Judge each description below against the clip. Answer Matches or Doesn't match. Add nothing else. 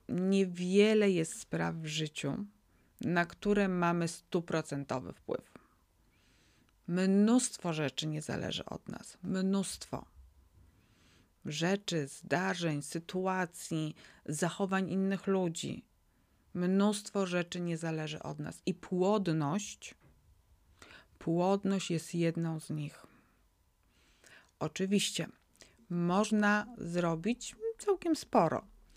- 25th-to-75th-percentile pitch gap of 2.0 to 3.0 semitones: Doesn't match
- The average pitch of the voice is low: Doesn't match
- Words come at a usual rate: Doesn't match